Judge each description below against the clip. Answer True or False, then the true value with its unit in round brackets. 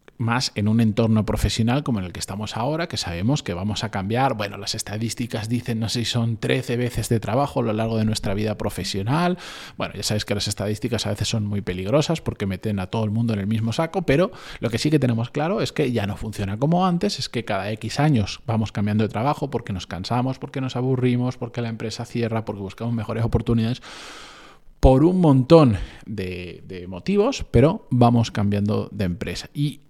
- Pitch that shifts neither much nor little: True (3.6 semitones)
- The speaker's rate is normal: False (215 wpm)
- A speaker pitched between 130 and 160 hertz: False (115 Hz)